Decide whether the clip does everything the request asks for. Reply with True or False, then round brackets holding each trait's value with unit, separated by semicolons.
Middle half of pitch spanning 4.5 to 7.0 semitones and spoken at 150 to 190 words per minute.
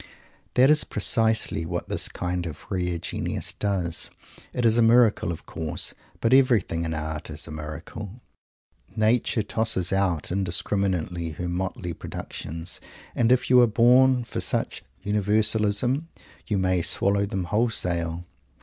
False (4.8 semitones; 140 wpm)